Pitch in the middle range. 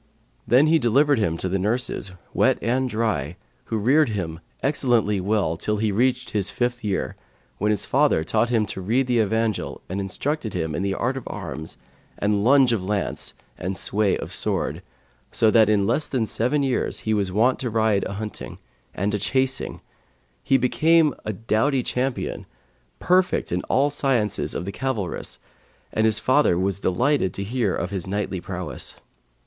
No: low, 110 Hz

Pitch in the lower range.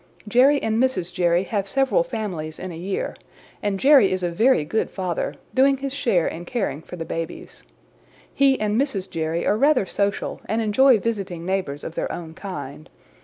No: high, 195 Hz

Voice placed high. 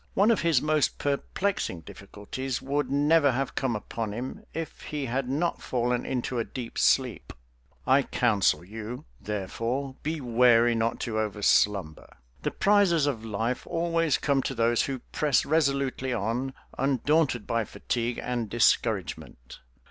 No: low, 125 Hz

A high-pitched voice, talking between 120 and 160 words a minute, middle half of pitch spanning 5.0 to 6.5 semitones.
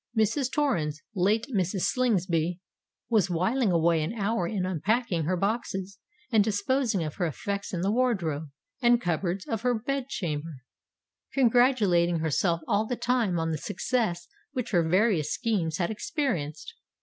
Yes: high, 195 Hz; average, 140 wpm; wide, 5.5 semitones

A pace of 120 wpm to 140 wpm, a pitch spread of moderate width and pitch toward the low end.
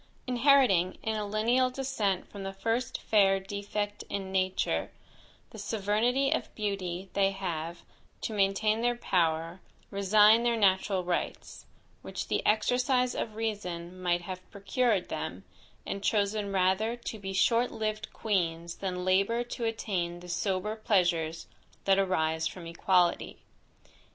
No: slow, 135 wpm; average, 3.2 semitones; high, 200 Hz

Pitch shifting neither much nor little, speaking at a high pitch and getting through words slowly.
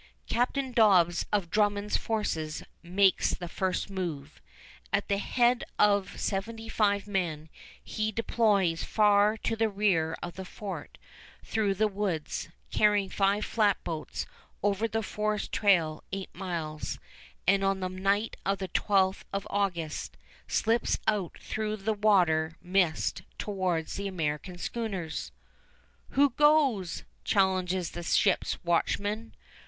Yes: average, 3.1 semitones; high, 195 Hz; slow, 125 wpm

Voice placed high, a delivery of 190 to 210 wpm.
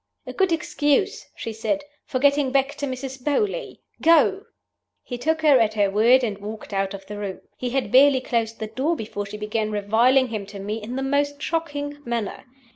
Yes: very high, 255 Hz; average, 200 wpm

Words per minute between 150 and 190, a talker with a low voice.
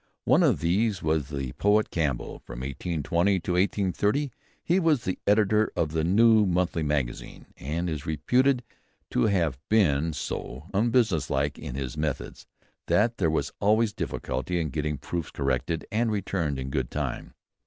Yes: average, 155 wpm; very low, 85 Hz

